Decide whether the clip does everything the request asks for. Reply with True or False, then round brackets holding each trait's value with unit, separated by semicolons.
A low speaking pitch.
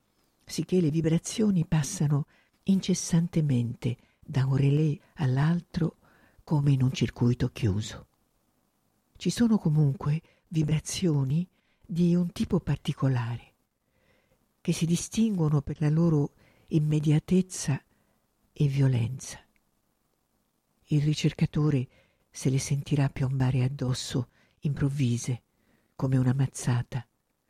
False (150 Hz)